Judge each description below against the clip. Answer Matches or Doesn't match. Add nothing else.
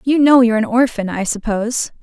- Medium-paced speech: Doesn't match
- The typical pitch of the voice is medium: Doesn't match